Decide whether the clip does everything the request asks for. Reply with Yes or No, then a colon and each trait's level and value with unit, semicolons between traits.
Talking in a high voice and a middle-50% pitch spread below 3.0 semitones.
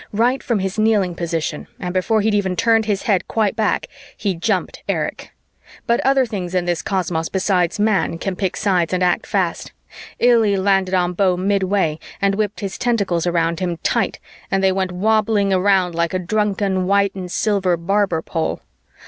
Yes: high, 195 Hz; narrow, 2.6 semitones